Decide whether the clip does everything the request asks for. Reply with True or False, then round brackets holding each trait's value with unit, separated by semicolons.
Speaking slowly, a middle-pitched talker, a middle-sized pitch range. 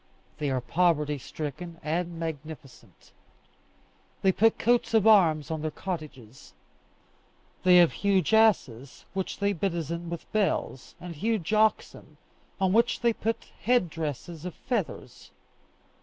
True (125 wpm; 175 Hz; 4.8 semitones)